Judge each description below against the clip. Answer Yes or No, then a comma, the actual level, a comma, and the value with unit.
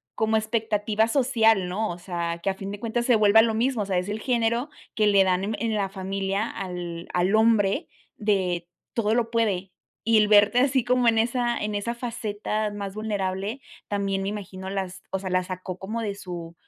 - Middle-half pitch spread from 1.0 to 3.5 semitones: Yes, average, 2.8 semitones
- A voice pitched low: No, high, 210 Hz